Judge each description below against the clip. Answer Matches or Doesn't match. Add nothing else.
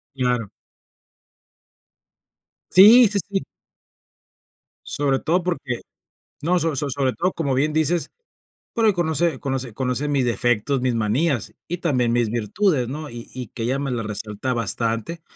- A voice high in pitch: Doesn't match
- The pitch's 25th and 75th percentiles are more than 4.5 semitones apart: Matches